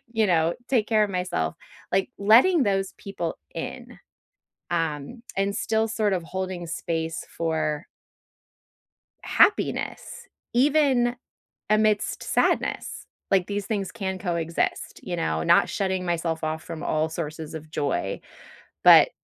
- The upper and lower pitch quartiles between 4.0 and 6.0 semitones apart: Yes, average, 4.8 semitones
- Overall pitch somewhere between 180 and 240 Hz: Yes, medium, 185 Hz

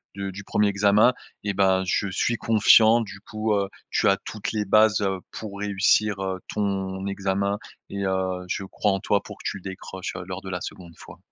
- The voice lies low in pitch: Yes, low, 100 Hz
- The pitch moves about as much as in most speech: No, narrow, 1.5 semitones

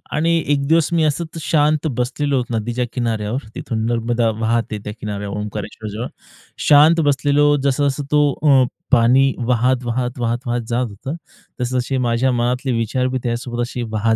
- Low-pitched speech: Yes, low, 125 Hz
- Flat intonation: No, average, 3.2 semitones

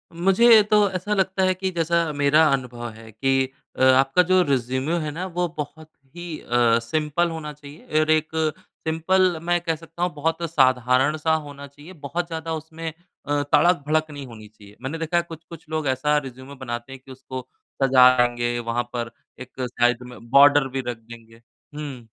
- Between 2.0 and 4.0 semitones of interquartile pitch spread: No, average, 4.5 semitones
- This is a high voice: No, medium, 145 Hz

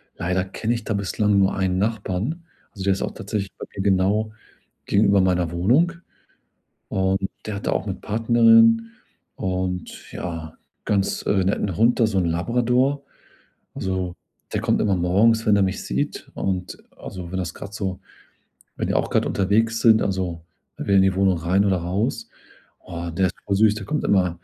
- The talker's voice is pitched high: No, very low, 95 Hz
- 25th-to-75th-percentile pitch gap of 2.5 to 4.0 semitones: Yes, average, 2.8 semitones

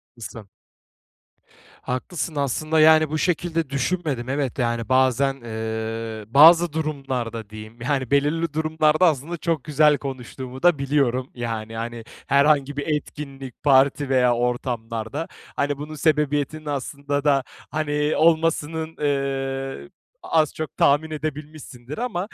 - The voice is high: No, medium, 140 Hz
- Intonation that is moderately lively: Yes, average, 3.6 semitones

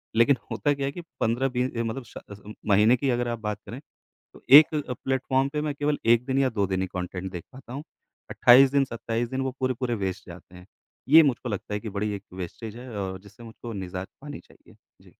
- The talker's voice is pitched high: No, low, 120 Hz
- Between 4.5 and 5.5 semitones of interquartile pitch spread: Yes, average, 4.8 semitones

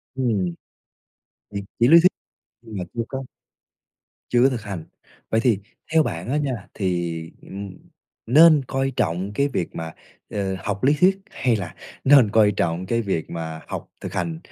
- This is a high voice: No, low, 105 Hz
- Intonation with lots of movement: Yes, wide, 6.5 semitones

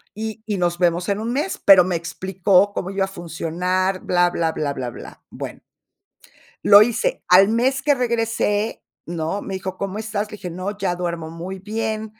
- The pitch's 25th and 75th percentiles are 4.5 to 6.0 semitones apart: No, average, 3.6 semitones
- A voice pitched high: Yes, high, 195 Hz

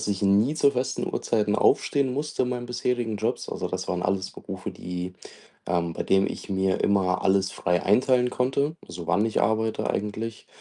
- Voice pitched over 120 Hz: No, low, 105 Hz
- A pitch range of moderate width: Yes, average, 4.7 semitones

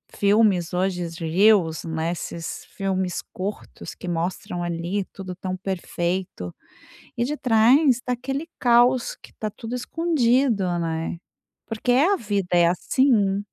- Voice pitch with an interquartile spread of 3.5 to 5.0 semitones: No, wide, 5.5 semitones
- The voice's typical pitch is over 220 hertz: No, high, 195 Hz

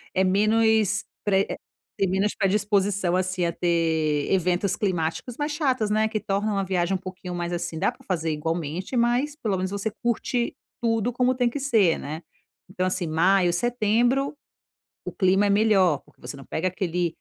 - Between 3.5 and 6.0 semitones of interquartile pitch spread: Yes, average, 4.0 semitones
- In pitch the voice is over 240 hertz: No, high, 195 Hz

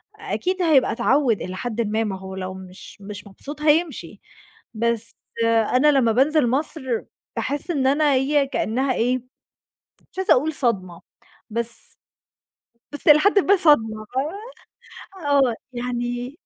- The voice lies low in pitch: No, very high, 255 Hz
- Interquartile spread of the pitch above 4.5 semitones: Yes, average, 4.9 semitones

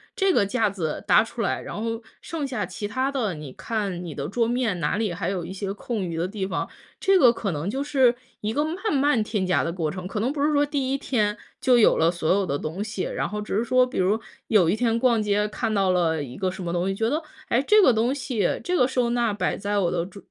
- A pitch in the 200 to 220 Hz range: Yes, high, 210 Hz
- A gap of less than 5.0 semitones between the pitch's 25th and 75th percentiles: No, wide, 5.4 semitones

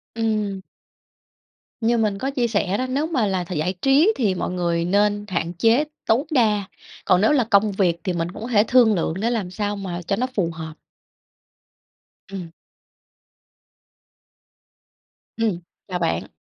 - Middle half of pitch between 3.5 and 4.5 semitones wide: Yes, average, 4.1 semitones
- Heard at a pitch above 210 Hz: No, high, 205 Hz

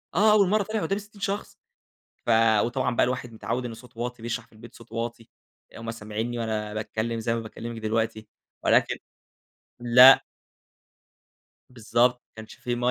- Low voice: Yes, low, 115 Hz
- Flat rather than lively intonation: Yes, narrow, 2.0 semitones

